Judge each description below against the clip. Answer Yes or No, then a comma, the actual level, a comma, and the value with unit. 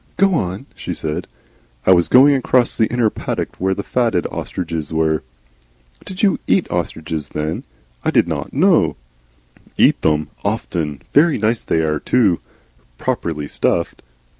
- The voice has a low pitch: Yes, very low, 90 Hz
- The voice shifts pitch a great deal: Yes, wide, 7.6 semitones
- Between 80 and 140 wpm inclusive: No, average, 150 wpm